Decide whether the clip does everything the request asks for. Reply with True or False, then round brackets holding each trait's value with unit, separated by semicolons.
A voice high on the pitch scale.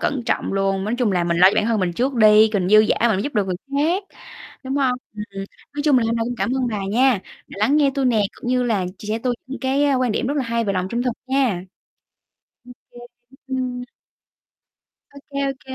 True (240 Hz)